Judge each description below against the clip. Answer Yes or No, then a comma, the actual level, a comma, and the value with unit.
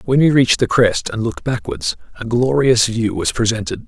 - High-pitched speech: No, low, 120 Hz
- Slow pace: No, average, 200 wpm